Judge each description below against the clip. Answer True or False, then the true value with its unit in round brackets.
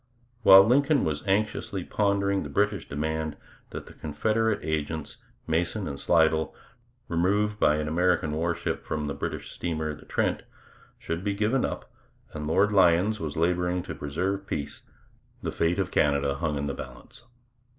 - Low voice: True (85 Hz)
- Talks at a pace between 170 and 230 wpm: False (155 wpm)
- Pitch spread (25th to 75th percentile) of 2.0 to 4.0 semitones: False (4.4 semitones)